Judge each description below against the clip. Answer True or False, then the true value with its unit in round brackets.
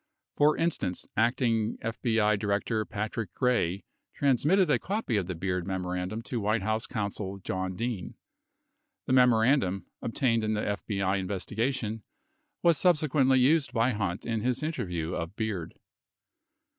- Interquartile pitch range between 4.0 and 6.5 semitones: True (4.6 semitones)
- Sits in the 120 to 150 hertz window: False (110 Hz)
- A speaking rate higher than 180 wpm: False (140 wpm)